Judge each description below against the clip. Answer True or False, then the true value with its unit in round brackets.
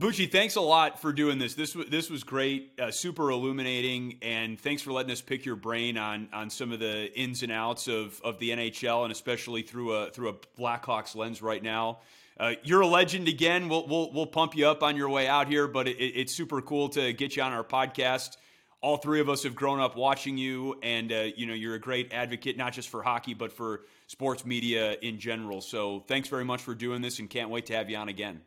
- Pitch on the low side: True (125 Hz)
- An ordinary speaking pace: False (240 wpm)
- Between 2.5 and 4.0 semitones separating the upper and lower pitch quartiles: True (3.6 semitones)